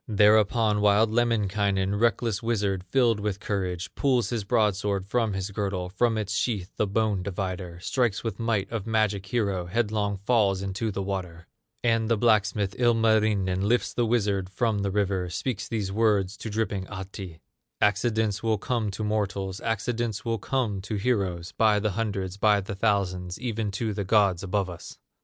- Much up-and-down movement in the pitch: No, narrow, 2.6 semitones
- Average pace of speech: Yes, average, 165 wpm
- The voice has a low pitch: Yes, low, 105 Hz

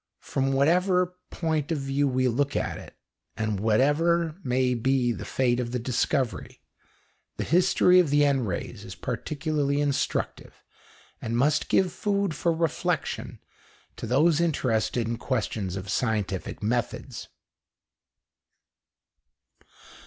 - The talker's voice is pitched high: No, low, 135 Hz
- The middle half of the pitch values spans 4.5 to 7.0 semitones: Yes, average, 5.1 semitones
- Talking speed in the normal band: No, slow, 125 wpm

